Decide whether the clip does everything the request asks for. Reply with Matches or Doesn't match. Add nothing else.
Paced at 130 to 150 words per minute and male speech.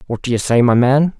Doesn't match